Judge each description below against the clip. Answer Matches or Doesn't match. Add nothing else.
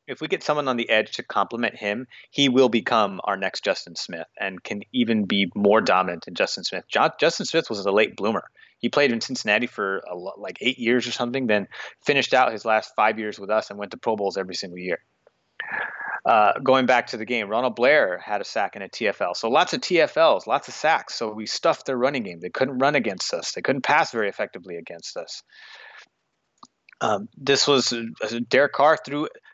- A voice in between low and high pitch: Doesn't match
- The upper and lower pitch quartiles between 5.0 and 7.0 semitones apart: Matches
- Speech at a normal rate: Doesn't match